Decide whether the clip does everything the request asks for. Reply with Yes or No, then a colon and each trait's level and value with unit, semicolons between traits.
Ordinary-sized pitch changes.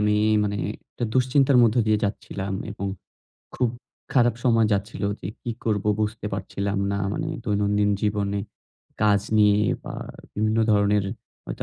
No: narrow, 1.6 semitones